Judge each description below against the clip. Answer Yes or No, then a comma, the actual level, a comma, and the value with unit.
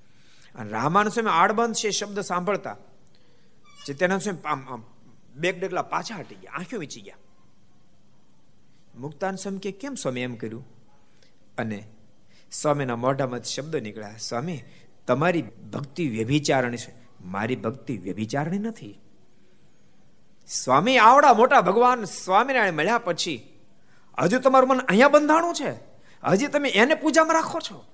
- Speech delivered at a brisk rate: No, average, 120 wpm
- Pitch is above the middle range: No, medium, 165 Hz